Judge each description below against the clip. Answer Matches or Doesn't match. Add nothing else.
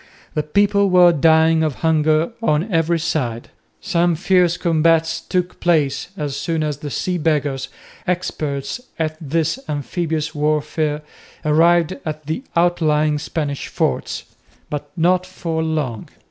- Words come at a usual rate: Doesn't match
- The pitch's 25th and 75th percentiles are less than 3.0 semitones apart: Matches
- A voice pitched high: Doesn't match